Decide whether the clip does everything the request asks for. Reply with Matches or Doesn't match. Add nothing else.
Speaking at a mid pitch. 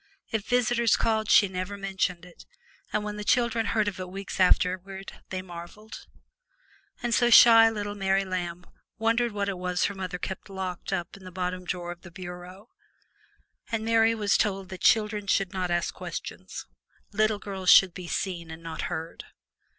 Doesn't match